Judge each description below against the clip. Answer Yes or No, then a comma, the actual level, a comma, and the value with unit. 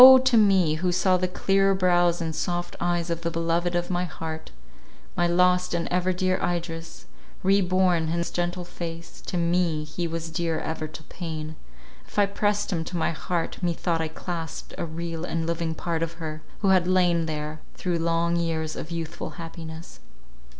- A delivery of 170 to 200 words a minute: Yes, average, 185 wpm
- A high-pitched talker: No, medium, 170 Hz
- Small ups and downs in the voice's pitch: Yes, narrow, 1.7 semitones